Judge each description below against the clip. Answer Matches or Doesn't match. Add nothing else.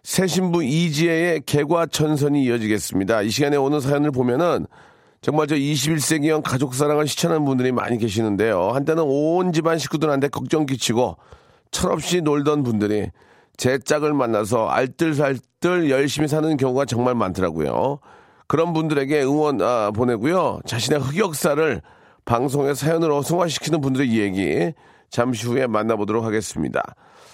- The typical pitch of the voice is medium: Matches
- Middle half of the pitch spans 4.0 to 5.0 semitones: Matches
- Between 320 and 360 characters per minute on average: Matches